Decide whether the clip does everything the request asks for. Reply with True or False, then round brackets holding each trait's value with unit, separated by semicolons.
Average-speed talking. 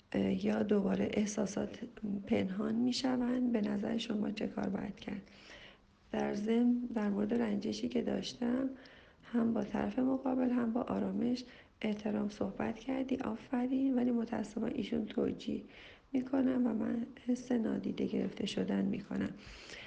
True (130 wpm)